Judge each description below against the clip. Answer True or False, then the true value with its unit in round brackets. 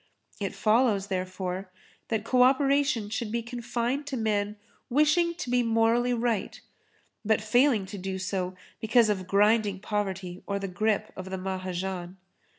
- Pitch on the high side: True (215 Hz)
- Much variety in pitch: False (4.1 semitones)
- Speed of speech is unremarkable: True (155 wpm)